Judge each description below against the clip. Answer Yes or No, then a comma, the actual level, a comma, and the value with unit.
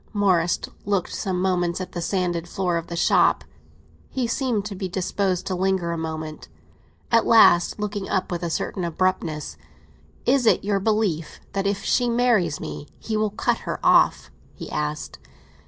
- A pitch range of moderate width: Yes, average, 3.3 semitones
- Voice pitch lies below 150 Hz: No, medium, 185 Hz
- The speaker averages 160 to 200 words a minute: Yes, average, 170 wpm